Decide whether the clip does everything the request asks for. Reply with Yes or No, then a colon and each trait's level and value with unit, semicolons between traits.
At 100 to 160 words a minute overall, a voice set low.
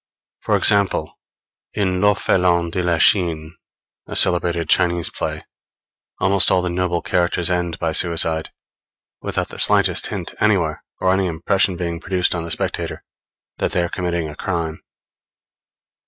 Yes: average, 140 wpm; very low, 85 Hz